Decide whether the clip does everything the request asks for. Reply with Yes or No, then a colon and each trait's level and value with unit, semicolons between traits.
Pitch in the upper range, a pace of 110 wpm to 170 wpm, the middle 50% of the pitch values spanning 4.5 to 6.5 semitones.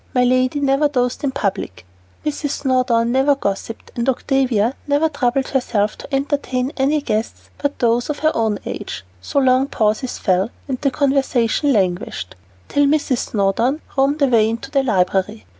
No: very high, 255 Hz; average, 155 wpm; average, 3.6 semitones